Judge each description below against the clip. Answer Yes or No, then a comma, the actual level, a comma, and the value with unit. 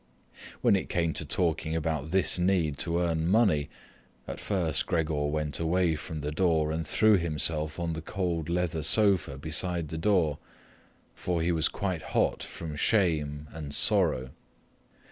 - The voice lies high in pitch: No, very low, 80 Hz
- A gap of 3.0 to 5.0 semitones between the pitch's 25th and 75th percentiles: No, narrow, 2.5 semitones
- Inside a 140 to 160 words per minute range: Yes, average, 155 wpm